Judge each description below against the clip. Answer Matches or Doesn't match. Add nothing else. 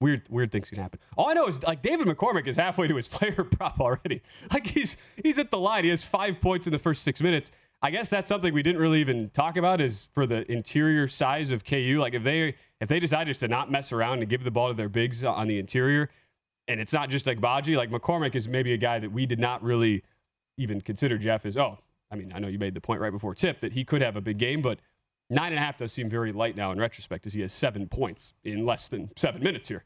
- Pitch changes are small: Doesn't match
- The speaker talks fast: Matches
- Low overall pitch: Matches